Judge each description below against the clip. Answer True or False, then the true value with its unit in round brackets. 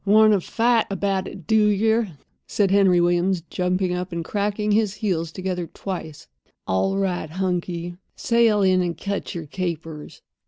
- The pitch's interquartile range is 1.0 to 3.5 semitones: True (2.8 semitones)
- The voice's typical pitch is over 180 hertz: True (190 Hz)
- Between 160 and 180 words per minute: False (145 wpm)